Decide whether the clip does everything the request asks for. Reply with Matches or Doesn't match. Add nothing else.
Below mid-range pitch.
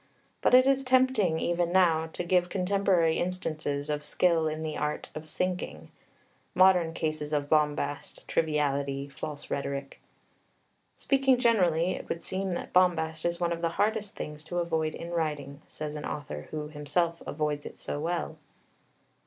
Doesn't match